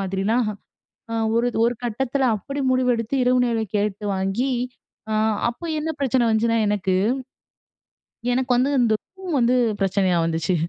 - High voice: Yes, high, 235 Hz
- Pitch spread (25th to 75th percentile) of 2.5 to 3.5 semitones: No, average, 4.0 semitones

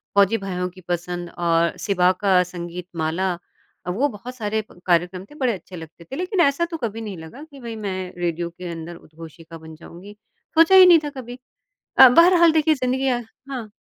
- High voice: Yes, high, 195 Hz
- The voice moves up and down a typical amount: No, wide, 6.8 semitones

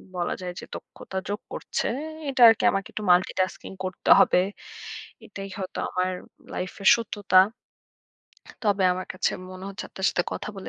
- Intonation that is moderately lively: No, narrow, 1.5 semitones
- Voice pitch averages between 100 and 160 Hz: No, high, 190 Hz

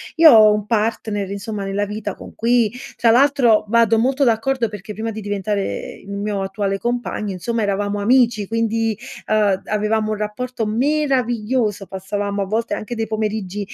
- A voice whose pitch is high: Yes, high, 215 Hz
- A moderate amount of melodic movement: No, narrow, 2.2 semitones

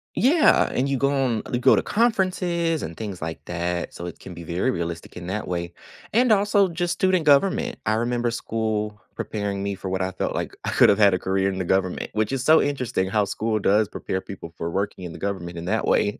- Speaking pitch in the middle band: No, low, 105 Hz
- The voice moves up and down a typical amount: No, wide, 7.1 semitones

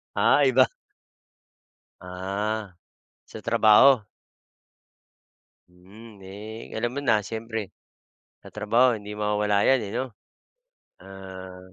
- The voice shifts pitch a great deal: No, average, 2.9 semitones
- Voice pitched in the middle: No, low, 105 Hz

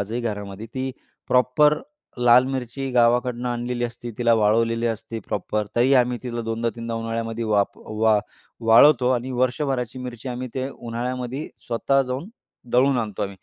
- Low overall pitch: Yes, low, 120 Hz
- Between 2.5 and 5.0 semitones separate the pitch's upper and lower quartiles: No, narrow, 1.9 semitones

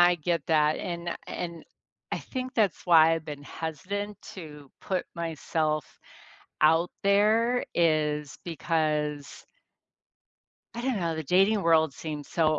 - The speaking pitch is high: No, medium, 165 Hz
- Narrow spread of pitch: No, average, 3.3 semitones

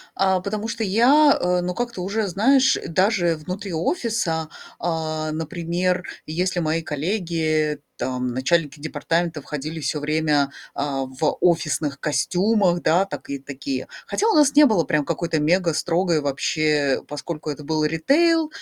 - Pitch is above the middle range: No, medium, 165 Hz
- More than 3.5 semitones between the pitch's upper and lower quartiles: Yes, average, 4.0 semitones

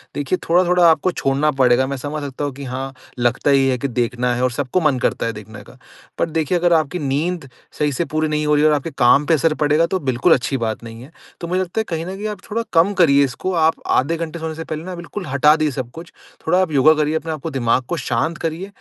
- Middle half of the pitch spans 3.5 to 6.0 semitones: Yes, average, 4.0 semitones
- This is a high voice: No, medium, 150 Hz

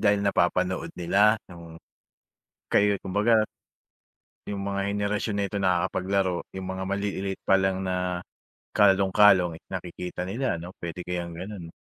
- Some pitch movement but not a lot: No, narrow, 2.0 semitones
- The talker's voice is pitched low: Yes, very low, 95 Hz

